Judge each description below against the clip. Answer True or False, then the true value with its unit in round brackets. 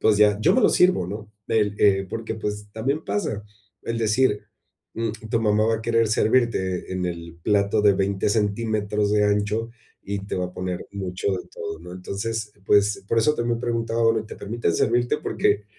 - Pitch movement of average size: False (2.3 semitones)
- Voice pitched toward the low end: True (105 Hz)